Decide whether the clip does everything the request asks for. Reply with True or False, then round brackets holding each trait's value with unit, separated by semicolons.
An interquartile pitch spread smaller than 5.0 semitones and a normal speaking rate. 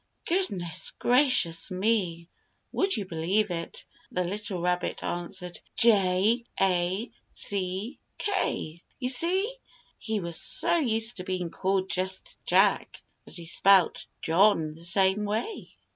False (4.2 semitones; 125 wpm)